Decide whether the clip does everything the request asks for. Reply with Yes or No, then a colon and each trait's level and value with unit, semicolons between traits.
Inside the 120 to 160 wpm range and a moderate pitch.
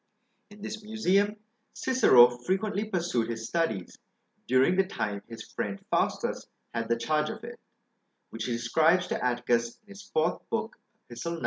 Yes: average, 155 wpm; medium, 155 Hz